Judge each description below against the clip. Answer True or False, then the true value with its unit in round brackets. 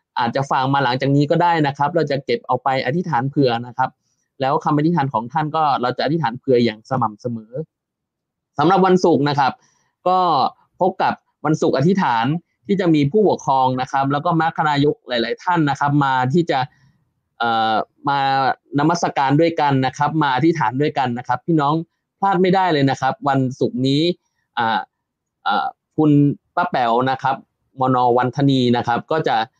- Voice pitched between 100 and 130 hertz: False (140 Hz)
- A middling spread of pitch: True (3.7 semitones)